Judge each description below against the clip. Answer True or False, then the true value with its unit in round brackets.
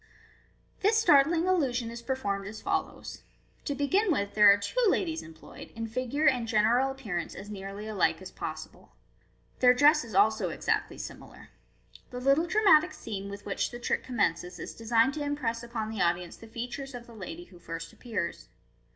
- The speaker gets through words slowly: False (175 wpm)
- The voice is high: True (230 Hz)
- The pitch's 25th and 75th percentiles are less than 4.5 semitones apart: False (5.5 semitones)